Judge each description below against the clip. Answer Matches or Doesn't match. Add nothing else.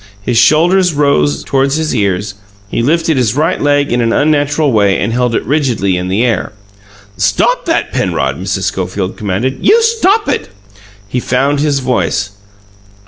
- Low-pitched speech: Matches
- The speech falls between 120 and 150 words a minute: Doesn't match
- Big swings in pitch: Matches